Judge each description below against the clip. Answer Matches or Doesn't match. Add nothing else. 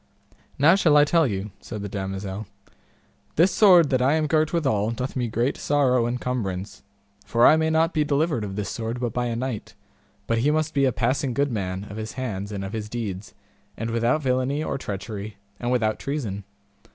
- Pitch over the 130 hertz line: Doesn't match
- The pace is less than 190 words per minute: Doesn't match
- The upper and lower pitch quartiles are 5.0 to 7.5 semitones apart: Matches